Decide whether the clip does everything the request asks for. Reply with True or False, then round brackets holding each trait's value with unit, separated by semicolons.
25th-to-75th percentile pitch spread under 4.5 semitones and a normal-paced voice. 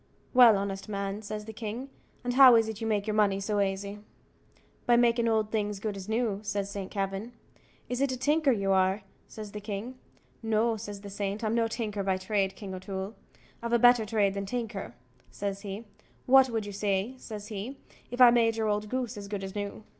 False (2.7 semitones; 215 wpm)